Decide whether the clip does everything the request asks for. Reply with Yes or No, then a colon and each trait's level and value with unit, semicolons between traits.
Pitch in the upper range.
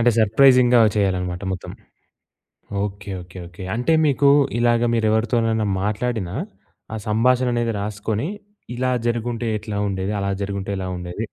No: low, 110 Hz